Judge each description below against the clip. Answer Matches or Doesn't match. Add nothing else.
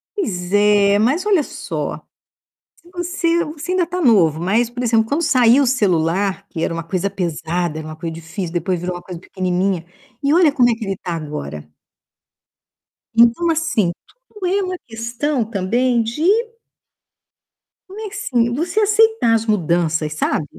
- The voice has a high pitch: Matches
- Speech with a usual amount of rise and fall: Doesn't match